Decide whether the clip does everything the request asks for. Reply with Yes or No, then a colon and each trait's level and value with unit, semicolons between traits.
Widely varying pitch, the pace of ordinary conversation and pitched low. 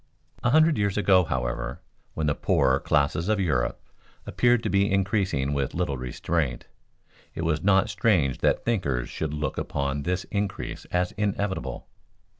Yes: wide, 6.2 semitones; average, 150 wpm; very low, 90 Hz